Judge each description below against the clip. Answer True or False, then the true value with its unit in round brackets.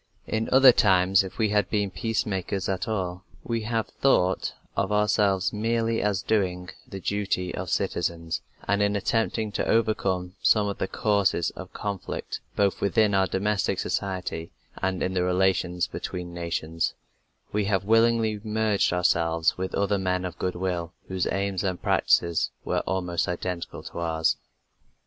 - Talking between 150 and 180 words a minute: True (155 wpm)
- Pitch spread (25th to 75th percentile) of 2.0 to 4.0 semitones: True (2.6 semitones)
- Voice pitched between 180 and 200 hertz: False (95 Hz)